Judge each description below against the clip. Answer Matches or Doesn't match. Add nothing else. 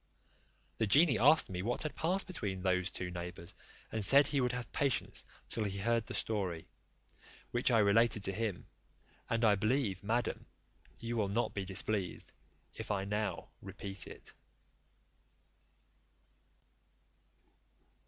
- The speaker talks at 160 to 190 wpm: Doesn't match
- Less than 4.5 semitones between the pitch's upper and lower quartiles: Matches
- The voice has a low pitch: Matches